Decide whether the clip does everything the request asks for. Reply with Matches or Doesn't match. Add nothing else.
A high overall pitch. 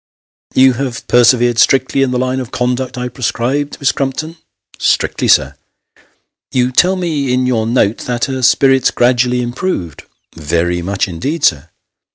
Doesn't match